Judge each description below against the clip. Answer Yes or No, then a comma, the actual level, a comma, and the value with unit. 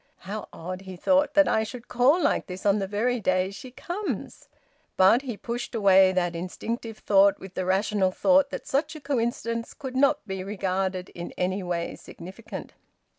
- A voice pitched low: No, high, 205 Hz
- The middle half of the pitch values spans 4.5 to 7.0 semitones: Yes, average, 4.8 semitones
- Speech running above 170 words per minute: Yes, average, 180 wpm